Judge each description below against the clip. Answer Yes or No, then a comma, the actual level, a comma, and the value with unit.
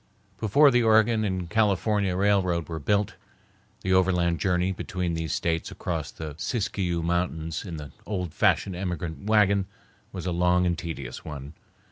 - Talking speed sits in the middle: Yes, average, 150 wpm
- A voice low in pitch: Yes, very low, 90 Hz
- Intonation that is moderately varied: Yes, average, 3.2 semitones